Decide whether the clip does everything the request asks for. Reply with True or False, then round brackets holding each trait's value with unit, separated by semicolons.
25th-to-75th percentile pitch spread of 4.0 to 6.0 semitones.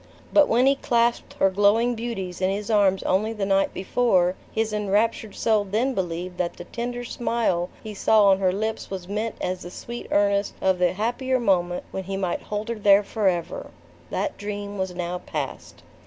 False (3.3 semitones)